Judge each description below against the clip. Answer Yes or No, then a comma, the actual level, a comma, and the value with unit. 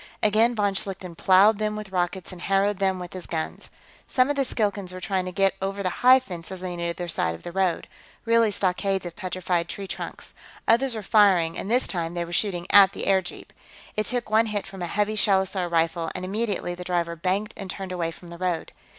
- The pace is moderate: No, fast, 220 wpm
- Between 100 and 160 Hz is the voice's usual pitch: No, high, 190 Hz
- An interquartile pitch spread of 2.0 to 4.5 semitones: Yes, average, 2.8 semitones